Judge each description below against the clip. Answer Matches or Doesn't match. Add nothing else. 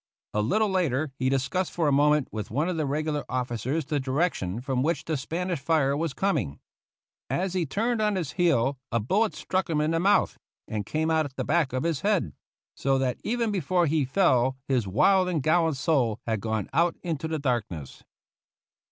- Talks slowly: Doesn't match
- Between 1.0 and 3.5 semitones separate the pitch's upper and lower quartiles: Doesn't match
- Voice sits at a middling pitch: Matches